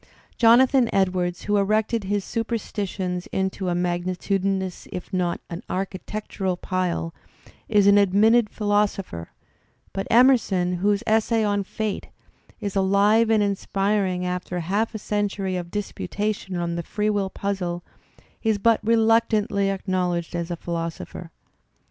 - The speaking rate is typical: No, slow, 125 wpm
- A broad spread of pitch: No, average, 2.7 semitones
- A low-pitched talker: No, high, 195 Hz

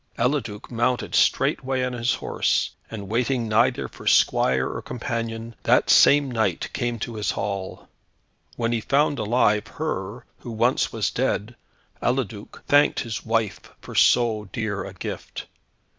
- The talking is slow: No, average, 145 wpm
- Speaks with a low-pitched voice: Yes, low, 115 Hz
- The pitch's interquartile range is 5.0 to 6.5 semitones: No, average, 2.8 semitones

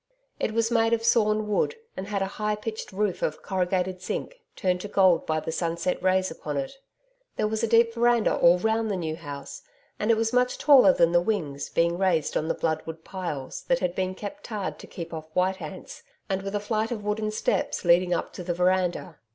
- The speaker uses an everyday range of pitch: Yes, average, 4.0 semitones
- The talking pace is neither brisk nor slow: No, fast, 215 wpm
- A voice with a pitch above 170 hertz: Yes, high, 190 Hz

